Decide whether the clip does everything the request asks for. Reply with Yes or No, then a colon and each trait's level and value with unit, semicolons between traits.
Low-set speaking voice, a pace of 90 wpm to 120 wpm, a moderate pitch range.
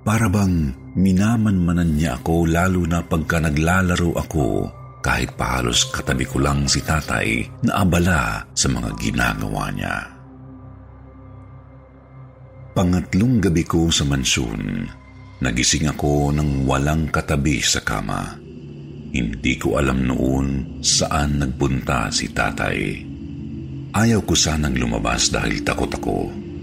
Yes: very low, 80 Hz; average, 115 wpm; average, 5.0 semitones